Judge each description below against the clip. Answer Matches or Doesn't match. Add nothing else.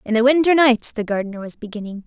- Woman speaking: Matches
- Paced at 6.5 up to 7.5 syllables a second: Matches